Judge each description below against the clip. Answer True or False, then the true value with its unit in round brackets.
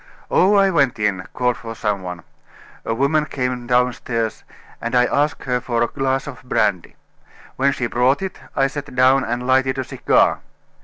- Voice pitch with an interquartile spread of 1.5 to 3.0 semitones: True (2.7 semitones)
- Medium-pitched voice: False (125 Hz)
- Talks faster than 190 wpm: False (175 wpm)